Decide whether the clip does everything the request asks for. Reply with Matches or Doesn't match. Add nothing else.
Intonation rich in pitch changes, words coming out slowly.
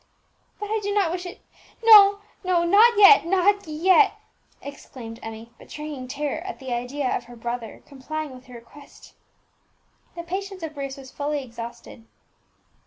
Doesn't match